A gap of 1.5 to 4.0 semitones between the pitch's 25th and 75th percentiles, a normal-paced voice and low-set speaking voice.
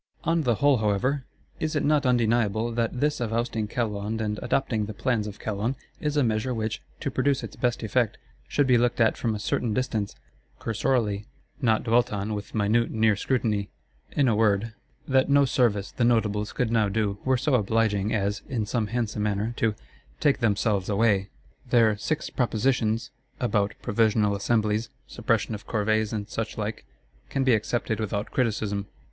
Yes: average, 2.7 semitones; average, 170 wpm; low, 110 Hz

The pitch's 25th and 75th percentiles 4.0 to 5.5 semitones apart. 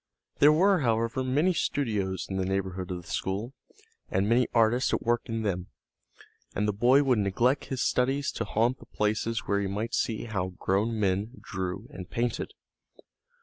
Yes: average, 4.4 semitones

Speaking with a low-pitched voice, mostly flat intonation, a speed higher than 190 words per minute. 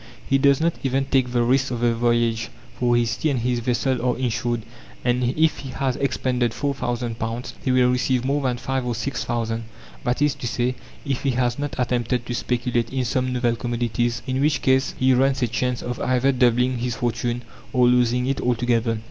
Yes: low, 125 Hz; narrow, 1.6 semitones; fast, 205 wpm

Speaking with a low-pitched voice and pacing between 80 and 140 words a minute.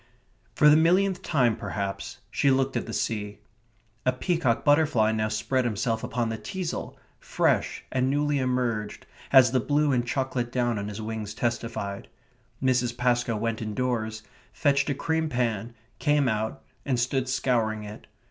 No: low, 125 Hz; average, 155 wpm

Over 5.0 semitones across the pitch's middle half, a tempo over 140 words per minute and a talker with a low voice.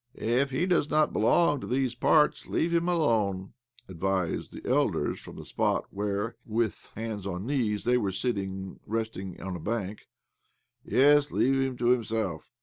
Yes: wide, 5.4 semitones; average, 165 wpm; low, 115 Hz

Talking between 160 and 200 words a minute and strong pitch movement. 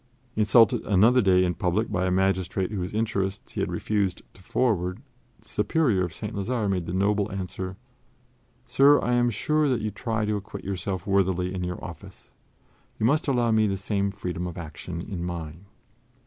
No: average, 180 wpm; average, 3.0 semitones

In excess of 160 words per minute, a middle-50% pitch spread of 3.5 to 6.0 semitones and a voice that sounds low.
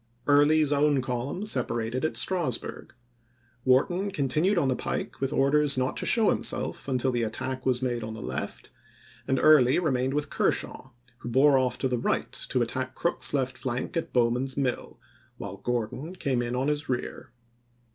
No: average, 175 wpm; average, 2.9 semitones; low, 130 Hz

